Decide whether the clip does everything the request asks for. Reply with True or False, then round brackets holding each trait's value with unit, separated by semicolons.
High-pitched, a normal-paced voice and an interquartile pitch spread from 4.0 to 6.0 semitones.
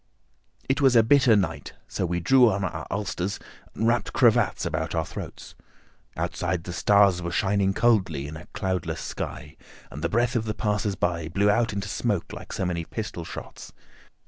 False (100 Hz; 180 wpm; 4.4 semitones)